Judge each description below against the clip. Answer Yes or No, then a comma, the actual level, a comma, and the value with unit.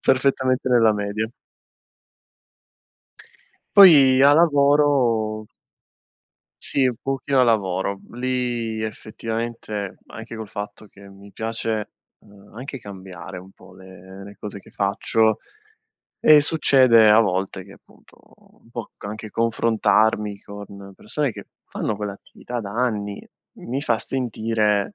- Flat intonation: No, average, 3.7 semitones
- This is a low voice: Yes, low, 110 Hz